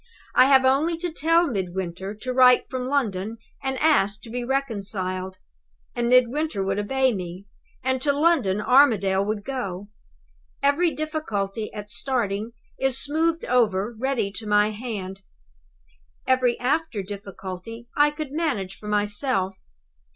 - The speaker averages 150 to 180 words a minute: No, slow, 135 wpm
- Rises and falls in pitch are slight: No, wide, 5.4 semitones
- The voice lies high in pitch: Yes, high, 235 Hz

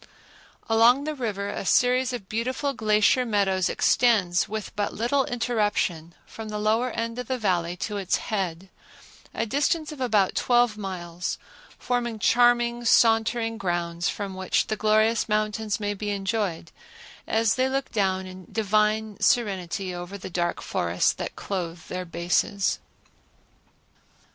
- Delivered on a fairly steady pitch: No, average, 3.9 semitones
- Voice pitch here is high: Yes, high, 215 Hz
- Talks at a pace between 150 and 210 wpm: No, average, 140 wpm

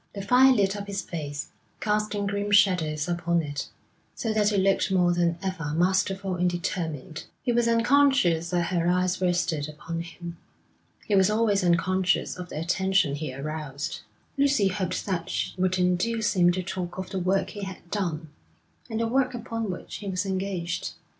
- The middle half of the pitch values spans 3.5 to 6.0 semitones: No, average, 3.0 semitones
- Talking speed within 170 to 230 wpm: Yes, average, 175 wpm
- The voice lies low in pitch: No, medium, 185 Hz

